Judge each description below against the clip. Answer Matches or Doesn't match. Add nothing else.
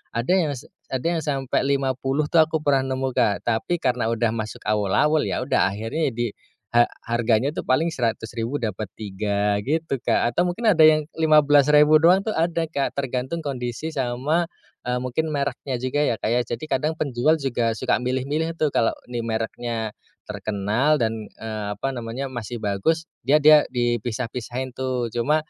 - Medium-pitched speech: Doesn't match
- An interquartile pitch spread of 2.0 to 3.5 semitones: Doesn't match